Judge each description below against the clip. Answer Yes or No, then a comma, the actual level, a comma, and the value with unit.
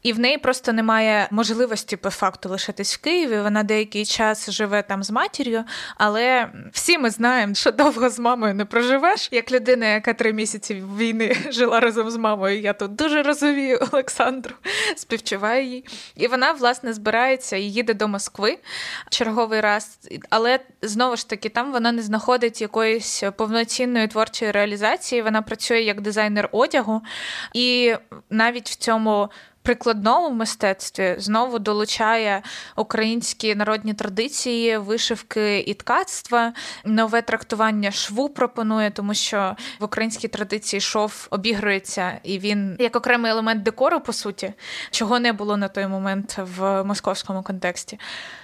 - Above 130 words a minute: Yes, average, 140 wpm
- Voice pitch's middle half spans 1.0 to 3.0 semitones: Yes, narrow, 2.5 semitones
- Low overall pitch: No, high, 225 Hz